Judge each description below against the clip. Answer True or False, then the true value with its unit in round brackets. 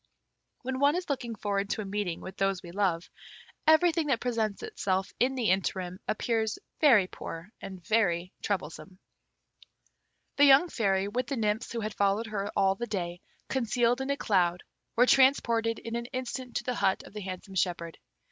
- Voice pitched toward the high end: True (215 Hz)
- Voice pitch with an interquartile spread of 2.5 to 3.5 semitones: False (4.5 semitones)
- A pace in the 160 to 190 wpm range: True (175 wpm)